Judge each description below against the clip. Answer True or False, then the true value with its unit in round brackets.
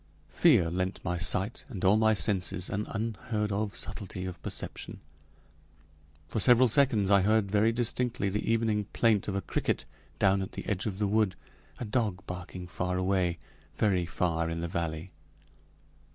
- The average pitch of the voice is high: False (100 Hz)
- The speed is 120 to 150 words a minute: False (165 wpm)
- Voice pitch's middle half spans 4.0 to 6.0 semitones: False (3.1 semitones)